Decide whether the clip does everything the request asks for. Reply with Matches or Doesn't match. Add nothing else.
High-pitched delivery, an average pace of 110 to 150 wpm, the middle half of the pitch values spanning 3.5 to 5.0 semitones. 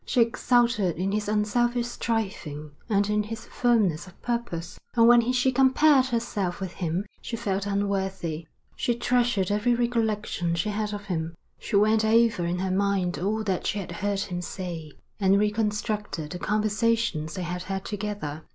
Doesn't match